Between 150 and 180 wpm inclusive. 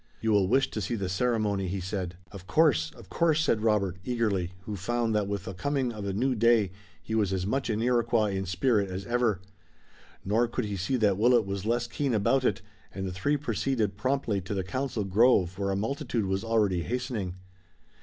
No: fast, 205 wpm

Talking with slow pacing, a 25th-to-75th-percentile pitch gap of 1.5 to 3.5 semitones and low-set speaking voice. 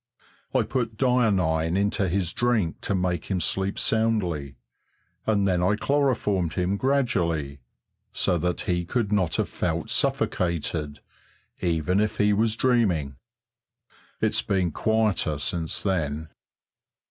No: slow, 125 wpm; average, 4.7 semitones; very low, 95 Hz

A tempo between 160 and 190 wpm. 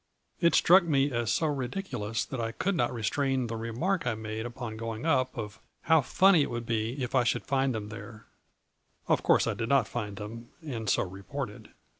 No: fast, 205 wpm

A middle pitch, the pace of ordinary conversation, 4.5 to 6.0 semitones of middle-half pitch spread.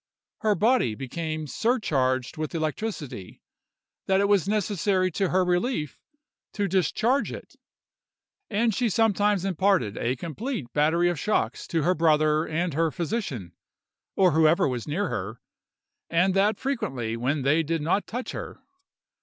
Yes: medium, 170 Hz; average, 145 wpm; average, 5.3 semitones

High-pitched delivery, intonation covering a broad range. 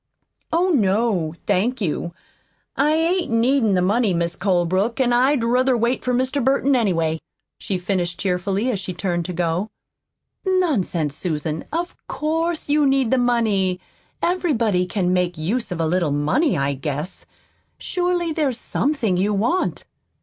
Yes: high, 215 Hz; wide, 7.0 semitones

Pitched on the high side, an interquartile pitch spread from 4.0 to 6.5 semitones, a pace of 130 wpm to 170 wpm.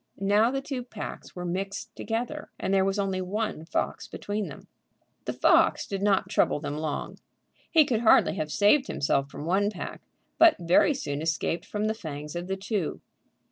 No: high, 195 Hz; average, 4.3 semitones; average, 180 wpm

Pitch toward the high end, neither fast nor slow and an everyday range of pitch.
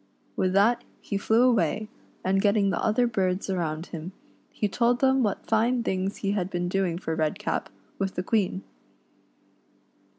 Yes: high, 195 Hz; average, 160 wpm; average, 3.3 semitones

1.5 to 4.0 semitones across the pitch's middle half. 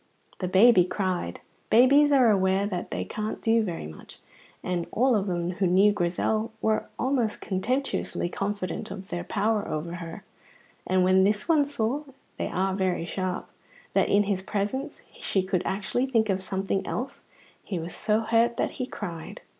Yes: average, 3.5 semitones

